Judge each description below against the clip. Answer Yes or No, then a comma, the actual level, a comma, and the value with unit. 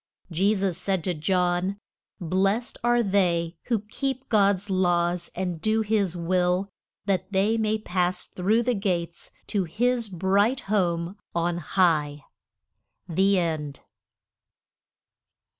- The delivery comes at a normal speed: No, slow, 120 wpm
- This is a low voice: No, high, 190 Hz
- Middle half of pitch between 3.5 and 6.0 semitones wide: No, average, 3.0 semitones